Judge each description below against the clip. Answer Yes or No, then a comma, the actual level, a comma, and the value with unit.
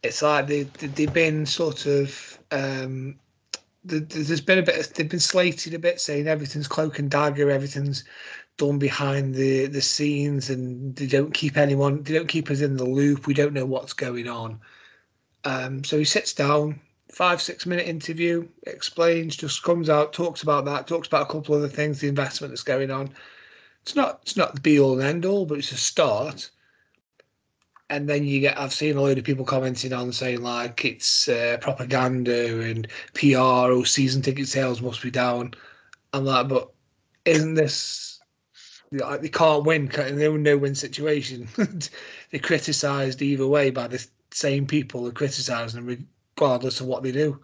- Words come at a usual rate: Yes, average, 180 wpm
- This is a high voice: No, medium, 140 Hz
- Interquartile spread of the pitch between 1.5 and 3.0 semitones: Yes, narrow, 2.4 semitones